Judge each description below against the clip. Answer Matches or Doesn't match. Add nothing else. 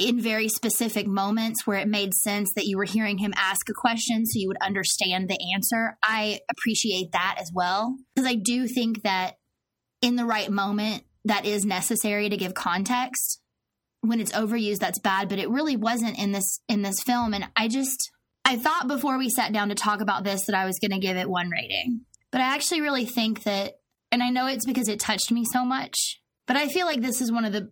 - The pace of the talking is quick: Matches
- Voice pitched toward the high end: Matches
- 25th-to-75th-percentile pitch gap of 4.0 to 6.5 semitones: Doesn't match